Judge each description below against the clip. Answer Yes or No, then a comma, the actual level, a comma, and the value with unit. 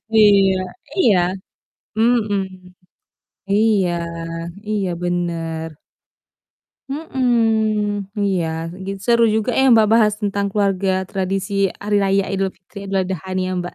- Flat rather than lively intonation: Yes, narrow, 2.3 semitones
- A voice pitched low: No, high, 200 Hz